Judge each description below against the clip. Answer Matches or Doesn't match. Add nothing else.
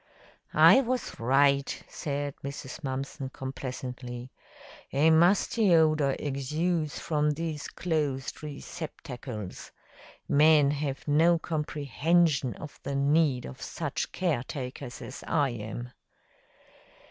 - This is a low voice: Doesn't match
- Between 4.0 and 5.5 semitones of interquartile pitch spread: Doesn't match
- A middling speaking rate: Doesn't match